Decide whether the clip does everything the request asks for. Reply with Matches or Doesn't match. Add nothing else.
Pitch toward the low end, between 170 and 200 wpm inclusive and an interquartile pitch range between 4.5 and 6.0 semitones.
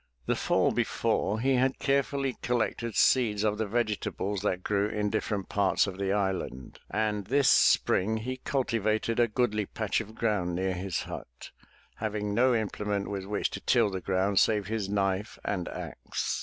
Doesn't match